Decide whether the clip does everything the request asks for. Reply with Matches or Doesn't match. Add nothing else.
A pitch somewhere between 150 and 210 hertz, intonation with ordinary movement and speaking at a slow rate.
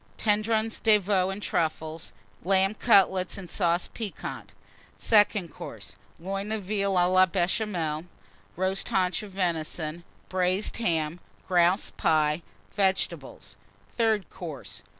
Matches